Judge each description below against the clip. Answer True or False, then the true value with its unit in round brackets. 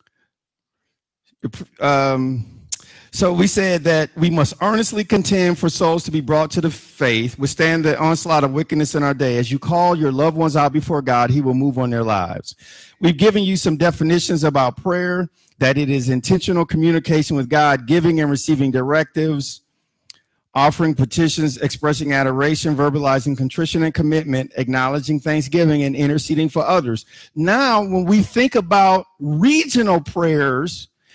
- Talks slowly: False (150 wpm)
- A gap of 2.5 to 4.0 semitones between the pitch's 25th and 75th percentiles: True (3.6 semitones)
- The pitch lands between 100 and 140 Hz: False (155 Hz)